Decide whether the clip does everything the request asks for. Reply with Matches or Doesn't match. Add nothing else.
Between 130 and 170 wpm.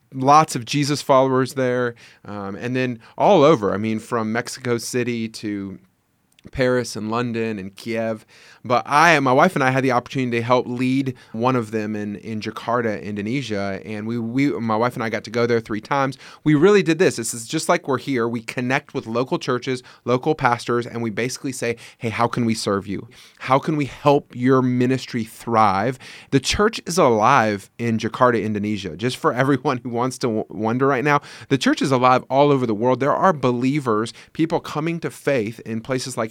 Doesn't match